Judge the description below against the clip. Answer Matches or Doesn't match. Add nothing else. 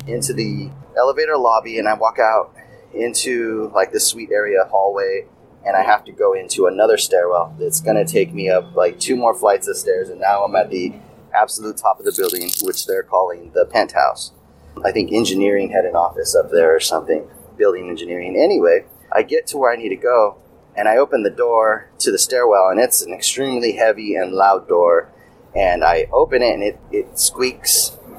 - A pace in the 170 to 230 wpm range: Matches